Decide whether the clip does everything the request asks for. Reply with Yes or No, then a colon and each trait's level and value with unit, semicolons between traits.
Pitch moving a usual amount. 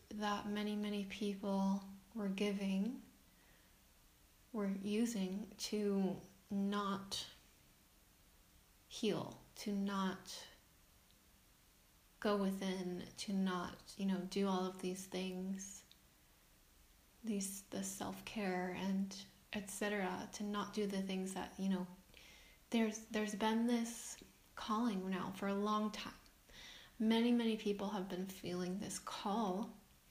No: narrow, 1.9 semitones